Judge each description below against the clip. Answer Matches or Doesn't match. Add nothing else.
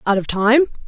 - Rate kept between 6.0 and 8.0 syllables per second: Doesn't match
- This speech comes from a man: Doesn't match